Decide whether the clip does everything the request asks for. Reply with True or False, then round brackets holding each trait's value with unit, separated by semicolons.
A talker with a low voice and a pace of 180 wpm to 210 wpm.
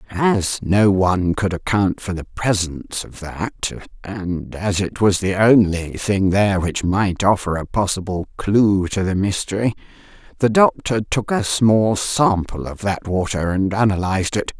False (100 Hz; 160 wpm)